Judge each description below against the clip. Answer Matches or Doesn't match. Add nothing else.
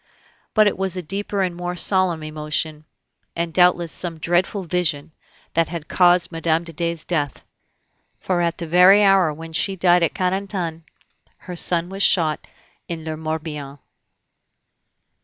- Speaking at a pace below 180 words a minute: Matches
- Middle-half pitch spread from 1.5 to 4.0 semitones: Matches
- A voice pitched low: Doesn't match